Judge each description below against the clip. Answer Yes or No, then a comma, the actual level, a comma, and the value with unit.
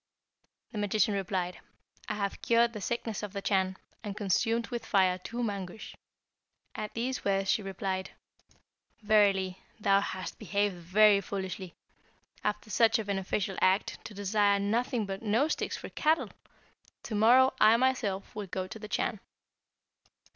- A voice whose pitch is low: No, high, 205 Hz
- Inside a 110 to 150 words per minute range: Yes, average, 145 wpm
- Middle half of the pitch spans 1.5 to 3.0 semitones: Yes, narrow, 2.4 semitones